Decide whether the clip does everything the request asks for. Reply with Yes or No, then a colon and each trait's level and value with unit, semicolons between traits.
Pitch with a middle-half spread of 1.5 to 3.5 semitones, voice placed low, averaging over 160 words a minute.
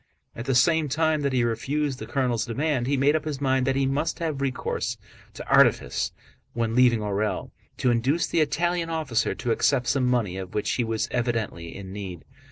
No: average, 4.0 semitones; low, 130 Hz; average, 195 wpm